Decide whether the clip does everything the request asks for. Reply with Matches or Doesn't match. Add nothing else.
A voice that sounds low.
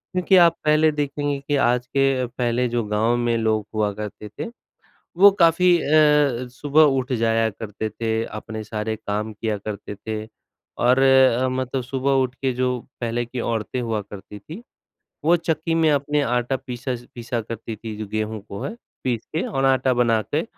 Matches